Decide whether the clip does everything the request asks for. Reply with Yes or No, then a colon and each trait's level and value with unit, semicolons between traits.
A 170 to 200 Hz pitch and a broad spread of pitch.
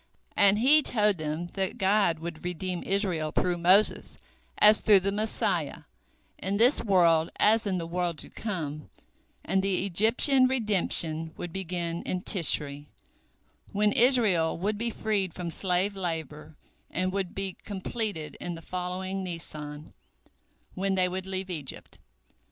No: medium, 185 Hz; average, 3.5 semitones